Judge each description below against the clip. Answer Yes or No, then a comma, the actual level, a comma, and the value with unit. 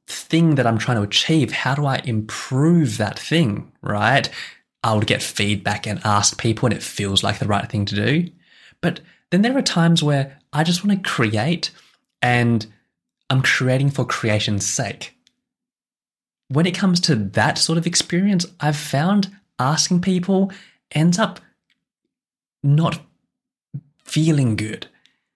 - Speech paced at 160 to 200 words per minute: No, average, 150 wpm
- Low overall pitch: No, medium, 150 Hz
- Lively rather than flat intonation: Yes, wide, 7.3 semitones